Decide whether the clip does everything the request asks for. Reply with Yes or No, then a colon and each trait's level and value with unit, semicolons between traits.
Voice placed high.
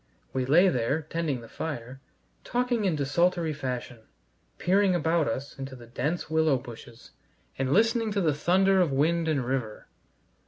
No: medium, 155 Hz